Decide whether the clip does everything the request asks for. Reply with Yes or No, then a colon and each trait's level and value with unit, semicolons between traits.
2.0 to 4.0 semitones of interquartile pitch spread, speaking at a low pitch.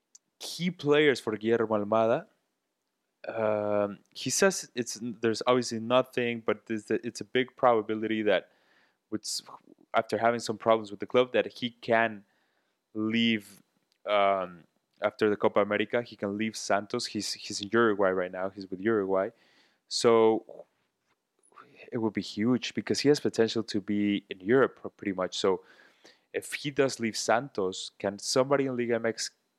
Yes: average, 2.8 semitones; low, 115 Hz